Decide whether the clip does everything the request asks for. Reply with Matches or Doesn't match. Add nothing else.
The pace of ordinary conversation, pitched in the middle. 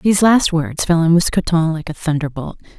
Matches